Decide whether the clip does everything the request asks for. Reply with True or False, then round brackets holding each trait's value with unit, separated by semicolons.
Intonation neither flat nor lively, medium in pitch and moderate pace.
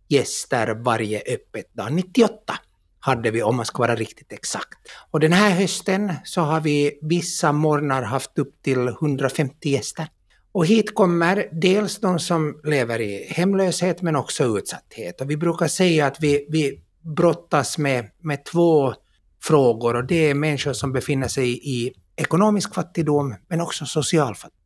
True (4.2 semitones; 155 Hz; 160 wpm)